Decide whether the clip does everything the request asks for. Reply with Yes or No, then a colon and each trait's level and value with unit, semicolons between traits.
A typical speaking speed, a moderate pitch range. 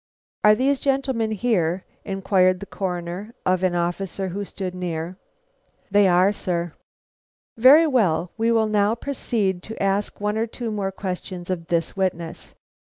Yes: average, 150 wpm; average, 3.5 semitones